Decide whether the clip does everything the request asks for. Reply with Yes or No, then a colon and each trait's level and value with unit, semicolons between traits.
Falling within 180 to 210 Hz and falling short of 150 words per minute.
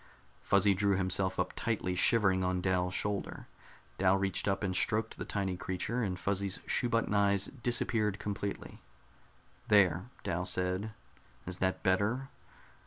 No: very low, 95 Hz; average, 140 wpm